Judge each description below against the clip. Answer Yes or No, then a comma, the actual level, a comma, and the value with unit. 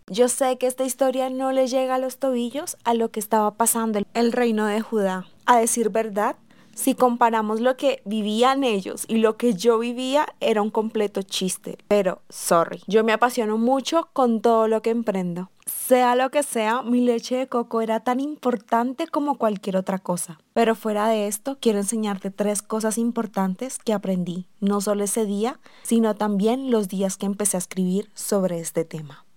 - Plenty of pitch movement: No, average, 3.2 semitones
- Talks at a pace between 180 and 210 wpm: Yes, average, 185 wpm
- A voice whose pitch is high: Yes, high, 225 Hz